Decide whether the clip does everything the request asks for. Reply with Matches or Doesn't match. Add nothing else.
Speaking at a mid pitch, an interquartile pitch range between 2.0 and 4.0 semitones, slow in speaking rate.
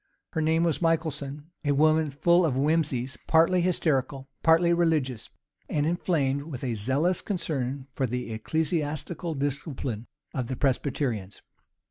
Matches